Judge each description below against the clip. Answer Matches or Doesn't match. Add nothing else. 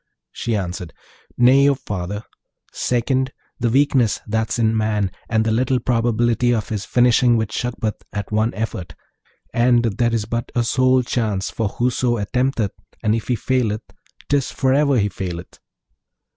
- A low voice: Matches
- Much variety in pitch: Doesn't match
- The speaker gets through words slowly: Doesn't match